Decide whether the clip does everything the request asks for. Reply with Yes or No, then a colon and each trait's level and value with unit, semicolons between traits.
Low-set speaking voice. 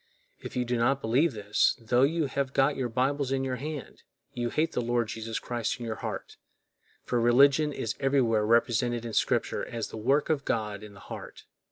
Yes: low, 120 Hz